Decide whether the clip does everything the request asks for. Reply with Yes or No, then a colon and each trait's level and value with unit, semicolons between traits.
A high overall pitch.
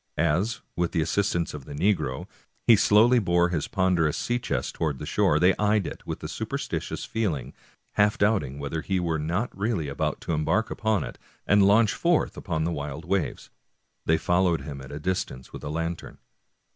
No: very low, 85 Hz